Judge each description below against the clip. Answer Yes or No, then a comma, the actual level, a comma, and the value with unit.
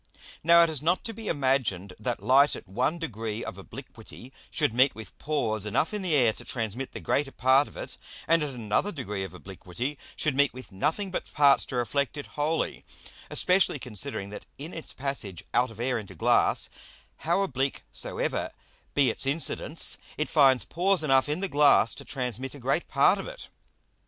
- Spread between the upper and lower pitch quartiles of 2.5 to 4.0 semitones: No, average, 4.7 semitones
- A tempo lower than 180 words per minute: No, average, 190 wpm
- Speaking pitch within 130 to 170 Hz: Yes, low, 135 Hz